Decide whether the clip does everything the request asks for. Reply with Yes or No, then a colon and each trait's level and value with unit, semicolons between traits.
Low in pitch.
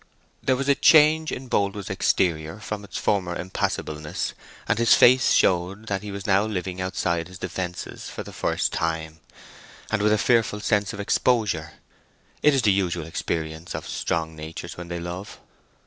Yes: very low, 95 Hz